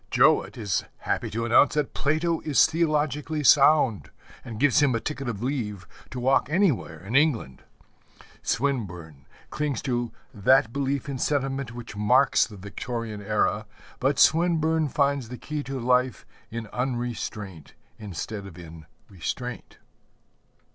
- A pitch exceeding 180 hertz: No, low, 125 Hz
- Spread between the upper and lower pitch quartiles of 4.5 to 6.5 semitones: Yes, average, 4.9 semitones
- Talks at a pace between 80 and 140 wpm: Yes, slow, 135 wpm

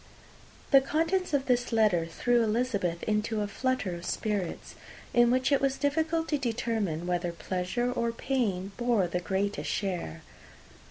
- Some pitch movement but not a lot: No, wide, 5.7 semitones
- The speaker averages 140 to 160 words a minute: Yes, average, 150 wpm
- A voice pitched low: No, high, 225 Hz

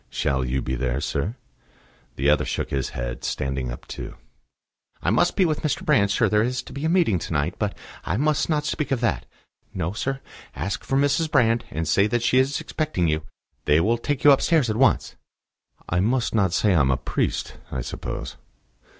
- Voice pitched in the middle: No, low, 105 Hz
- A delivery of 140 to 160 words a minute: No, fast, 205 wpm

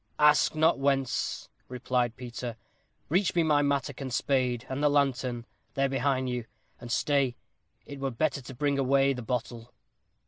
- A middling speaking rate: Yes, average, 165 wpm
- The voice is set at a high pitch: No, low, 135 Hz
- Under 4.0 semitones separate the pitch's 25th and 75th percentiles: Yes, narrow, 2.4 semitones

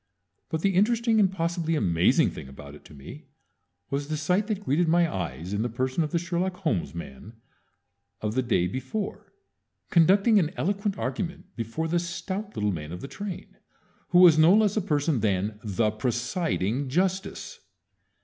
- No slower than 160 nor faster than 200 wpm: Yes, average, 170 wpm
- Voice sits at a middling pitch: Yes, medium, 155 Hz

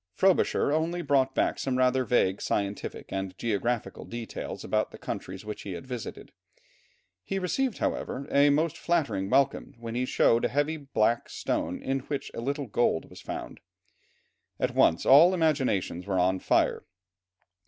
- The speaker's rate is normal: Yes, average, 155 wpm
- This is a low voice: Yes, low, 125 Hz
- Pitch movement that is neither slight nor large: No, wide, 5.9 semitones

